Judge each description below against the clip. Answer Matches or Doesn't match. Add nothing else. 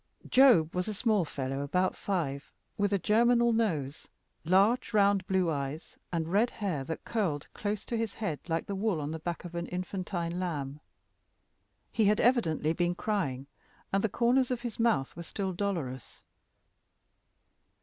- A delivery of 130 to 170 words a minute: Matches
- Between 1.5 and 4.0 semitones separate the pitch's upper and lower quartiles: Doesn't match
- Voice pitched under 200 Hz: Matches